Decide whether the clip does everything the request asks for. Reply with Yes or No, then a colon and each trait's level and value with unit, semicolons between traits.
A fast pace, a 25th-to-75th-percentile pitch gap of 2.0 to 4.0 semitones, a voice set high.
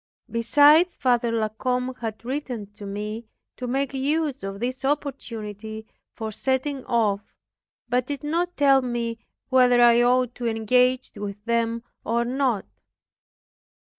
No: slow, 135 wpm; average, 3.0 semitones; high, 245 Hz